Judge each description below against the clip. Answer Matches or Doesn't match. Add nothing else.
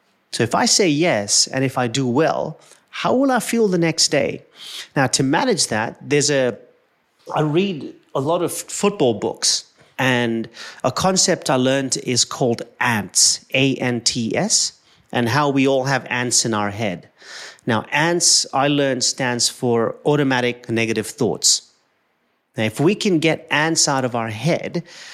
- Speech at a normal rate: Matches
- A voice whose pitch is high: Doesn't match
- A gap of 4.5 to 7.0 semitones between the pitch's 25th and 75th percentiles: Matches